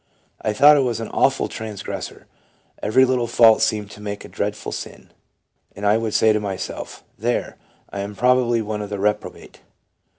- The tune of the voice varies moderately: No, narrow, 2.3 semitones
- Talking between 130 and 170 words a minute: No, average, 190 wpm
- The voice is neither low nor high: No, low, 110 Hz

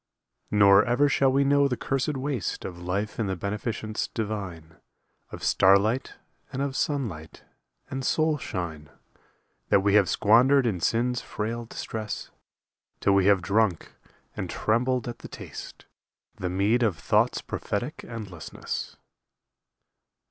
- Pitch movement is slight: No, average, 4.5 semitones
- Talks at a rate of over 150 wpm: No, slow, 135 wpm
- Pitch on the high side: No, low, 110 Hz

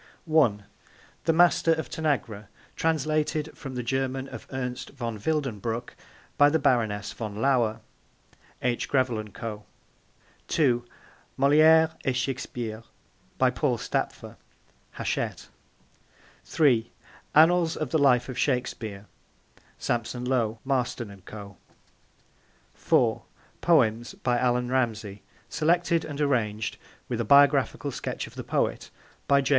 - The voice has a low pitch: Yes, low, 125 Hz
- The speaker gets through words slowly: Yes, slow, 120 wpm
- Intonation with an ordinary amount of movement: Yes, average, 4.3 semitones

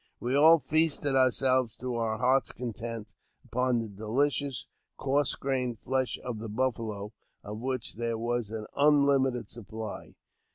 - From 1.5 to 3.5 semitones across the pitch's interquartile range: Yes, average, 2.9 semitones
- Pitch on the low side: Yes, low, 125 Hz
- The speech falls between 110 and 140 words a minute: Yes, slow, 135 wpm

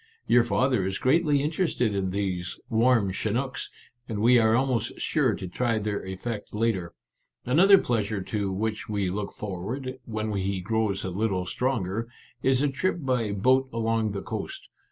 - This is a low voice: Yes, low, 110 Hz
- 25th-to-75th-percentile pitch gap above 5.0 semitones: No, average, 4.3 semitones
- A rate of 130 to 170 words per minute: Yes, average, 165 wpm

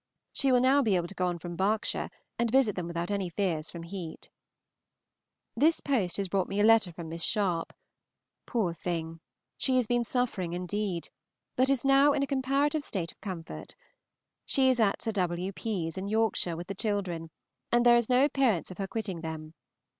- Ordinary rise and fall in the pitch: No, wide, 5.8 semitones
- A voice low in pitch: No, high, 200 Hz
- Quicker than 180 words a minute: Yes, average, 190 wpm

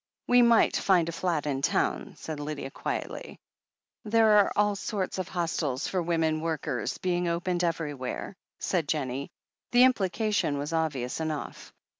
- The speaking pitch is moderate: Yes, medium, 165 Hz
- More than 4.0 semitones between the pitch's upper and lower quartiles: Yes, average, 4.4 semitones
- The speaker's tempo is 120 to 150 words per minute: Yes, average, 145 wpm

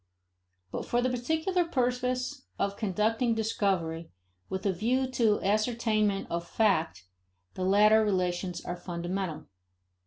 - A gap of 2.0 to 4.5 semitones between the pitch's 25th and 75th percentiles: No, average, 4.9 semitones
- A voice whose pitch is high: Yes, high, 210 Hz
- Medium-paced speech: No, slow, 120 wpm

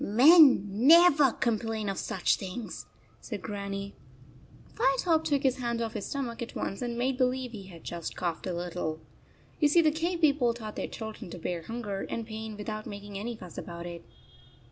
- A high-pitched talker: Yes, high, 225 Hz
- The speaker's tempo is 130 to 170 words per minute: No, average, 190 wpm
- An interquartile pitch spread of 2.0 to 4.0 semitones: No, average, 4.9 semitones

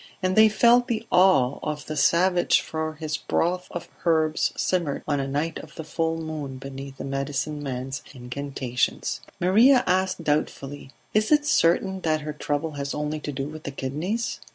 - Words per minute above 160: Yes, average, 170 wpm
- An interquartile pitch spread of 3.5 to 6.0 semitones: Yes, average, 4.4 semitones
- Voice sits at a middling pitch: Yes, medium, 155 Hz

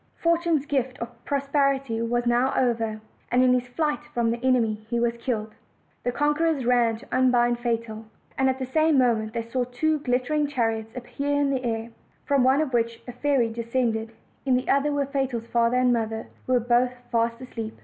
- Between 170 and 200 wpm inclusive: Yes, average, 195 wpm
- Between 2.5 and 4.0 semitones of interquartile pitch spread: Yes, average, 2.8 semitones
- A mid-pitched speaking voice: No, high, 245 Hz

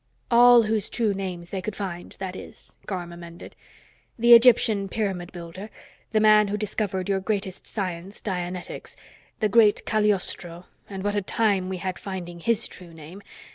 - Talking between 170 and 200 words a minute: No, average, 160 wpm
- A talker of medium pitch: No, high, 195 Hz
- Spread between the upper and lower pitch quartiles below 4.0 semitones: Yes, average, 2.9 semitones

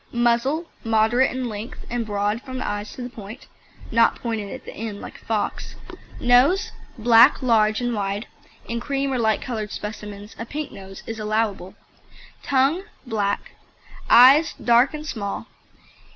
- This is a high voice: Yes, high, 230 Hz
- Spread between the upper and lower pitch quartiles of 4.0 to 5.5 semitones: No, average, 3.3 semitones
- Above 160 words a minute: No, average, 155 wpm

